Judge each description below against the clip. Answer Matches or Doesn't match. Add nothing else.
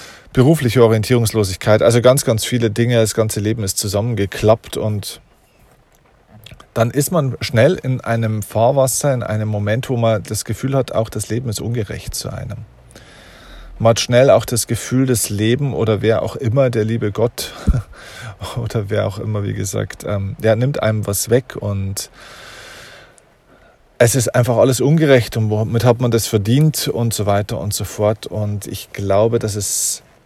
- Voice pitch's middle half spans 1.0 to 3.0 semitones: Matches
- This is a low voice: Matches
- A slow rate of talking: Doesn't match